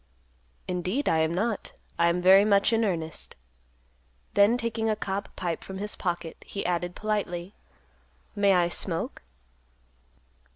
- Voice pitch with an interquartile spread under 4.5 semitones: Yes, average, 3.3 semitones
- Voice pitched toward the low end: No, high, 190 Hz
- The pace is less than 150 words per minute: Yes, slow, 135 wpm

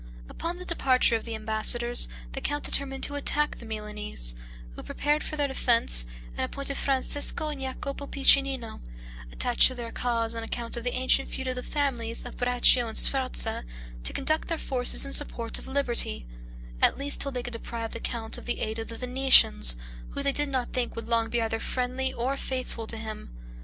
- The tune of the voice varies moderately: Yes, average, 3.2 semitones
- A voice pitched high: Yes, very high, 250 Hz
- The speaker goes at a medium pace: Yes, average, 195 wpm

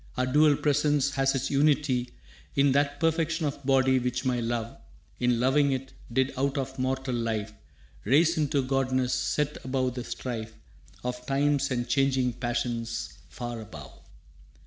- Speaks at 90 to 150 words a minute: Yes, average, 145 wpm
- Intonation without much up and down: Yes, narrow, 2.3 semitones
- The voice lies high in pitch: No, low, 130 Hz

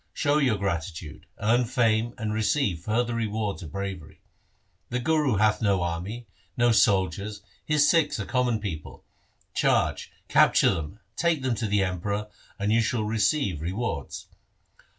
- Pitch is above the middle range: No, low, 105 Hz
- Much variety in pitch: No, average, 3.9 semitones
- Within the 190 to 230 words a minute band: No, average, 150 wpm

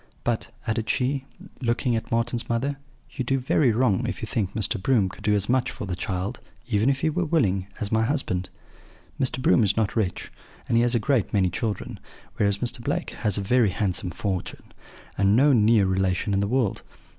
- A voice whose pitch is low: Yes, low, 110 Hz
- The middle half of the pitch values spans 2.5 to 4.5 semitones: Yes, average, 4.0 semitones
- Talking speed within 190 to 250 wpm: Yes, fast, 205 wpm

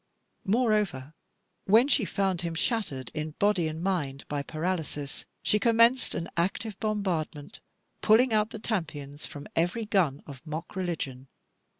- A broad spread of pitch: Yes, wide, 6.0 semitones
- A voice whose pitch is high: No, medium, 175 Hz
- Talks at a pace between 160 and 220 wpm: No, slow, 135 wpm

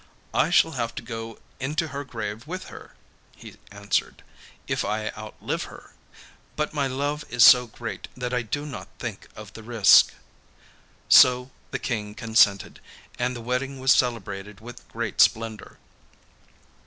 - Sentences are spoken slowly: No, average, 150 wpm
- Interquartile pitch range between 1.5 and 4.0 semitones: Yes, average, 3.2 semitones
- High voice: No, low, 120 Hz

